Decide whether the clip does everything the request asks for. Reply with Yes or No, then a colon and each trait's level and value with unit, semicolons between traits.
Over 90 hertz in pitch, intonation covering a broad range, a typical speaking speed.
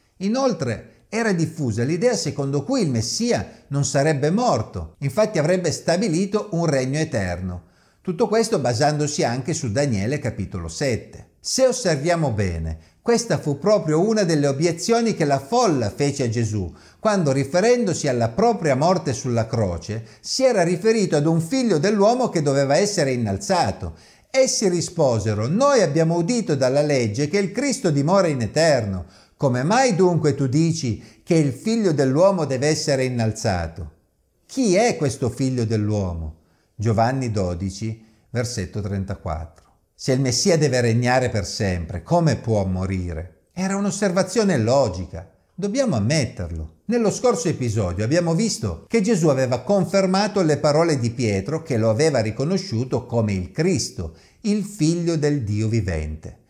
Yes: medium, 140 Hz; wide, 8.7 semitones; average, 140 wpm